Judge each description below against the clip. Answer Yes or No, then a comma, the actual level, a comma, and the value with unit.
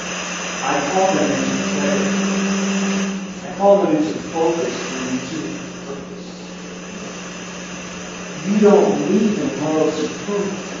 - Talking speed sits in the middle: No, slow, 105 wpm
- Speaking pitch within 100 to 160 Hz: No, high, 190 Hz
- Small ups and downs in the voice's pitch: No, average, 4.3 semitones